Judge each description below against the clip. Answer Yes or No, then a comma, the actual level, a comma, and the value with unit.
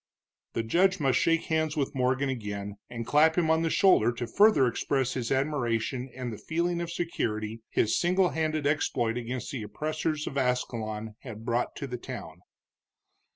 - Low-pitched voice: Yes, low, 130 Hz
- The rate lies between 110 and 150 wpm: No, average, 170 wpm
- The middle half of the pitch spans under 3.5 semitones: No, wide, 5.4 semitones